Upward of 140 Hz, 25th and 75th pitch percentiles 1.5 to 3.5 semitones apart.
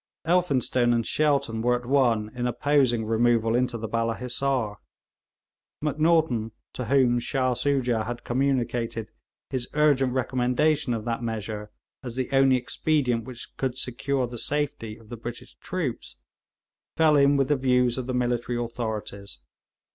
No: low, 125 Hz; average, 2.9 semitones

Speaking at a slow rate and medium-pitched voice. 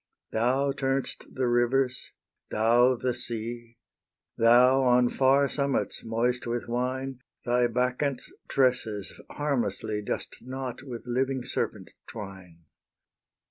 No: slow, 105 wpm; low, 125 Hz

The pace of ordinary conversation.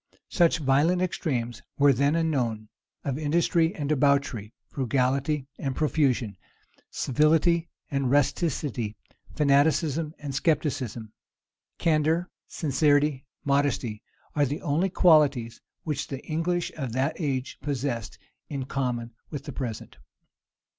No: slow, 110 wpm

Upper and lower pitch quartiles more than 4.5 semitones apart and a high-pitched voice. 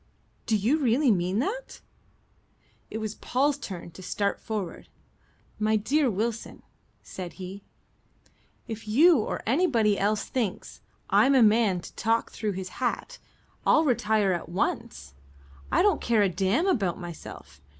Yes: average, 5.1 semitones; high, 215 Hz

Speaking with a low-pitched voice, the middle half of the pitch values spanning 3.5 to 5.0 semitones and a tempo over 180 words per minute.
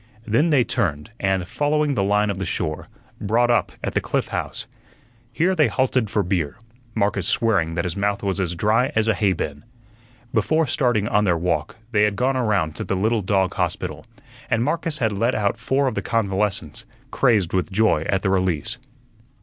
Yes: low, 105 Hz; average, 4.2 semitones; average, 190 wpm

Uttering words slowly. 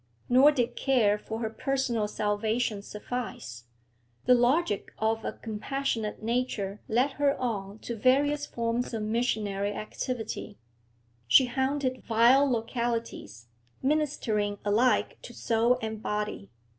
Yes: slow, 120 wpm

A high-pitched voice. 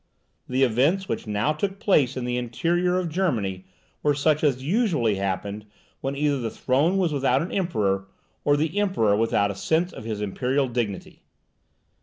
No: low, 135 Hz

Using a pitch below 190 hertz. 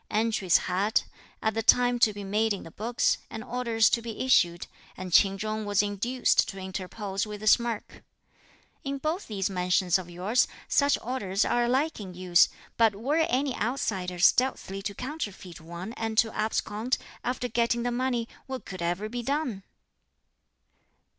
No: high, 220 Hz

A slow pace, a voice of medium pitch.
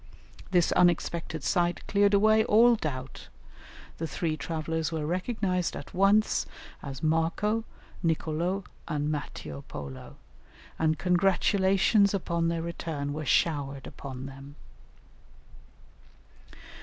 Yes: slow, 105 wpm; medium, 165 Hz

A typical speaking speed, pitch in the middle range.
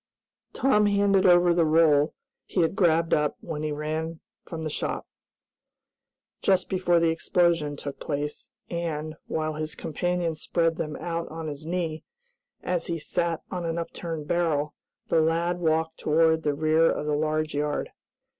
Yes: average, 155 wpm; medium, 160 Hz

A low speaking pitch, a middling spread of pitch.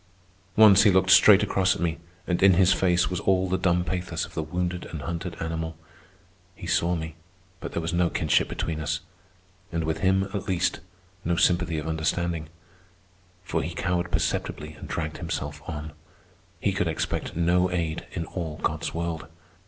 No: very low, 85 Hz; narrow, 2.2 semitones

